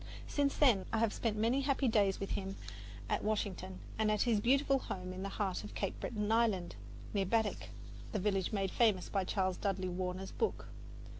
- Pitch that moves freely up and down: No, average, 3.1 semitones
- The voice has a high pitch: Yes, high, 205 Hz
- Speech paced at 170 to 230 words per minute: Yes, average, 190 wpm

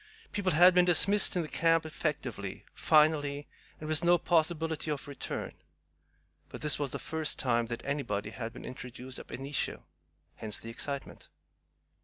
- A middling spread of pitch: Yes, average, 4.4 semitones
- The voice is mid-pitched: Yes, medium, 150 Hz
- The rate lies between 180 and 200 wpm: No, average, 150 wpm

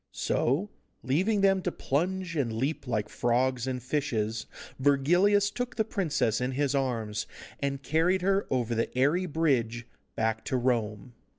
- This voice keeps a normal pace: Yes, average, 150 wpm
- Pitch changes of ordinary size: No, wide, 6.9 semitones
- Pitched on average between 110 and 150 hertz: Yes, low, 135 Hz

